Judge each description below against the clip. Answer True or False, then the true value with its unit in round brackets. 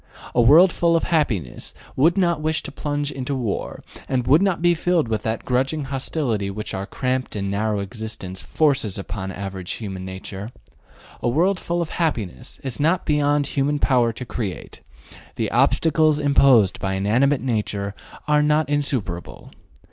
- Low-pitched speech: True (130 Hz)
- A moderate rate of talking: True (160 wpm)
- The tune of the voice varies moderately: False (6.5 semitones)